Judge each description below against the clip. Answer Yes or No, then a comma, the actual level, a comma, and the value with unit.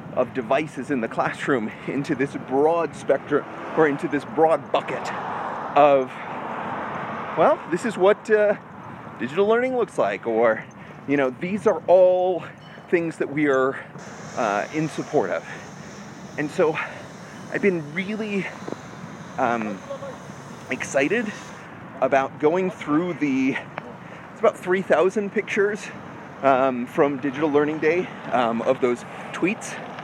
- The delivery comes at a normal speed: No, slow, 125 wpm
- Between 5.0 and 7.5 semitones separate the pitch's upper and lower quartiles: Yes, wide, 5.5 semitones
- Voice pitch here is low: No, medium, 175 Hz